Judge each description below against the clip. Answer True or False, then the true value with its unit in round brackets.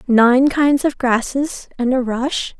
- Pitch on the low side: False (260 Hz)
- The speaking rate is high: False (160 wpm)